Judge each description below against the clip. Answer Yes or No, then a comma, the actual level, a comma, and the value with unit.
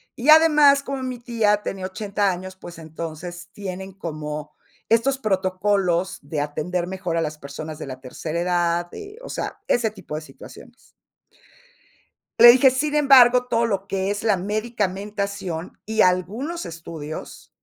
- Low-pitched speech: No, high, 190 Hz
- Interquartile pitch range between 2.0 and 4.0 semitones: No, wide, 5.4 semitones